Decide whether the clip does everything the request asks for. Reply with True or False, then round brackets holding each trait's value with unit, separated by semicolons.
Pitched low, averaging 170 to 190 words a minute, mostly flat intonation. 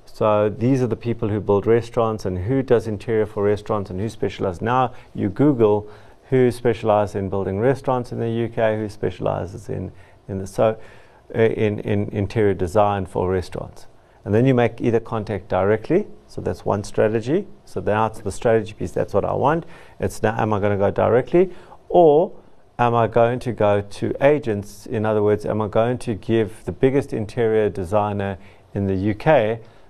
True (110 Hz; 180 wpm; 2.3 semitones)